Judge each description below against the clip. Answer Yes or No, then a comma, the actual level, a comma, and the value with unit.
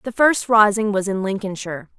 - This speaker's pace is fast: No, average, 180 wpm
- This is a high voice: Yes, high, 205 Hz